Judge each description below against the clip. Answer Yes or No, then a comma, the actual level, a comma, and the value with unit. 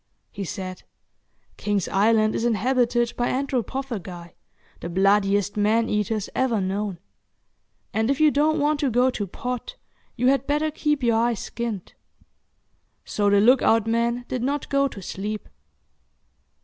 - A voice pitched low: No, high, 230 Hz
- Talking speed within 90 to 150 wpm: Yes, average, 145 wpm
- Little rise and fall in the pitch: No, average, 4.2 semitones